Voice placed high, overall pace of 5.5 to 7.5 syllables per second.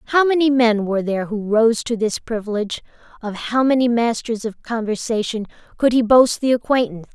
Yes: high, 230 Hz; 5.7 syllables/s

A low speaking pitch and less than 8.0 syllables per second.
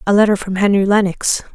No: high, 200 Hz; 6.0 syllables/s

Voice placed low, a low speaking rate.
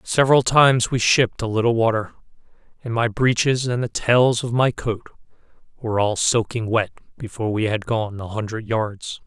No: low, 115 Hz; average, 175 wpm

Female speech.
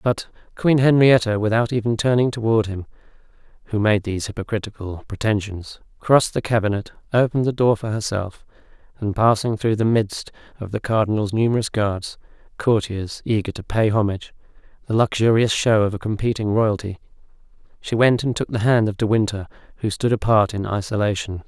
No: male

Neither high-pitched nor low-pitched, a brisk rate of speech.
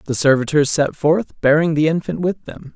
No: medium, 155 Hz; average, 195 wpm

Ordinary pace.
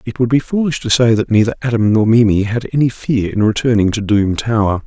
No: fast, 235 wpm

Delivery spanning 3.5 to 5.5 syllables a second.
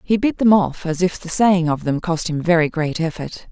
Yes: 5.0 syllables/s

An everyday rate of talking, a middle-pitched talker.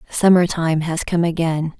Yes: average, 165 wpm; medium, 165 Hz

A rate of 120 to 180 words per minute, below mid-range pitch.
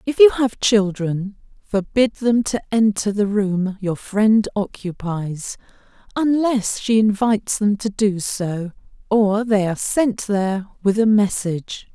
No: average, 140 wpm; high, 210 Hz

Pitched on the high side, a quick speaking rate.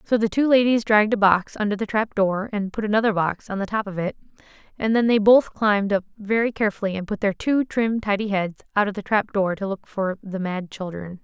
Yes: high, 205 Hz; fast, 245 wpm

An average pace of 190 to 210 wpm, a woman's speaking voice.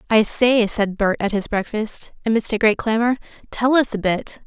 Yes: average, 200 wpm; female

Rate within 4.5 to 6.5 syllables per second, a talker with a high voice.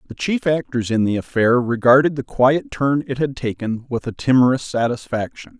No: 5.0 syllables/s; low, 125 Hz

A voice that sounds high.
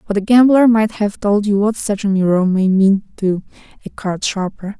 Yes: high, 205 Hz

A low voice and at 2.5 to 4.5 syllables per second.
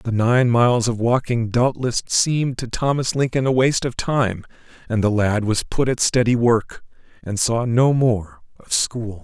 Yes: low, 120 Hz; 4.4 syllables/s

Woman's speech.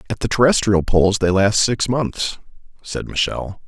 No: male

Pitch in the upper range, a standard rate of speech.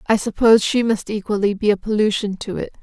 No: high, 210 Hz; fast, 210 wpm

